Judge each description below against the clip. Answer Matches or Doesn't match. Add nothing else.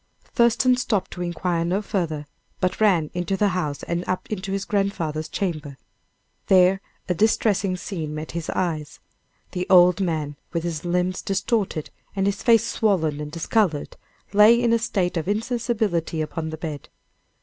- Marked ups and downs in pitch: Doesn't match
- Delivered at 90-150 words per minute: Doesn't match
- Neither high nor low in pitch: Matches